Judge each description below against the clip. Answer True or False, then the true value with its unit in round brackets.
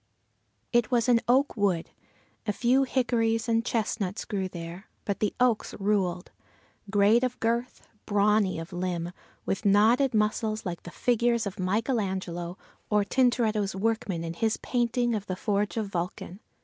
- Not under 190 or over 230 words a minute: False (150 wpm)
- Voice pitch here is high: True (210 Hz)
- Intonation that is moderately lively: True (3.7 semitones)